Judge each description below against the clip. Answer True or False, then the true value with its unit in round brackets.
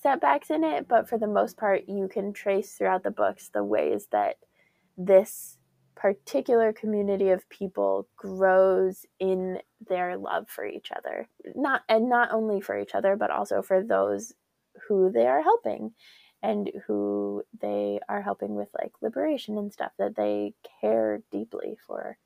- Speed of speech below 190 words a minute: True (160 wpm)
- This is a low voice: False (190 Hz)